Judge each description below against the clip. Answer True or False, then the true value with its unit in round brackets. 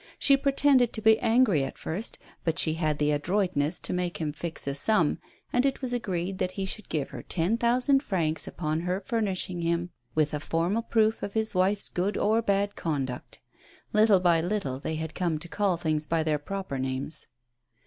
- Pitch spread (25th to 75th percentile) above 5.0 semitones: True (5.4 semitones)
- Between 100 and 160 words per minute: False (195 wpm)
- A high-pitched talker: False (180 Hz)